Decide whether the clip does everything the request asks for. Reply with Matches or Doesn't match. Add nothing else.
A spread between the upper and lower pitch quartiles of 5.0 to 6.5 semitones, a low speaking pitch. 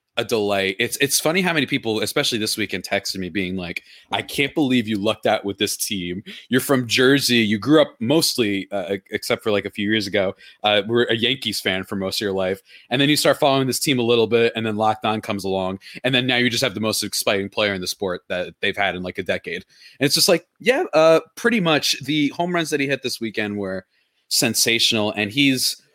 Matches